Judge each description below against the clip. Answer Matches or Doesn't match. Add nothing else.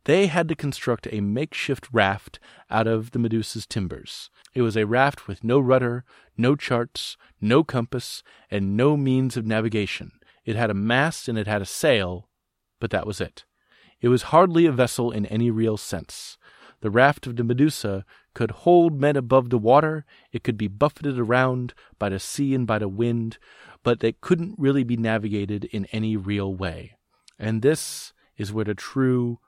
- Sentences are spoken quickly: Doesn't match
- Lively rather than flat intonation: Doesn't match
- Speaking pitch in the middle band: Doesn't match